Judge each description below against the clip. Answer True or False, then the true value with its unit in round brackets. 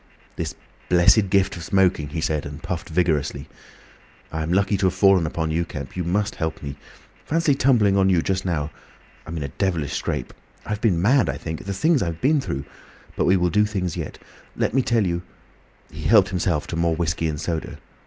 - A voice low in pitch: True (90 Hz)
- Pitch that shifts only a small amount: False (3.6 semitones)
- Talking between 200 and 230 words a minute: True (205 wpm)